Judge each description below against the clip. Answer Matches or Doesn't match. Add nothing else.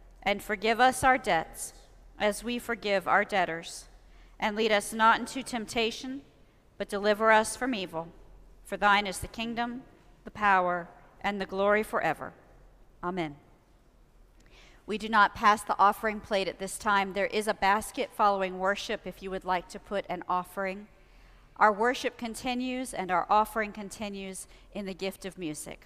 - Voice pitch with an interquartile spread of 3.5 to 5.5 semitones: Doesn't match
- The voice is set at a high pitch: Matches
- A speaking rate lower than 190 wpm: Matches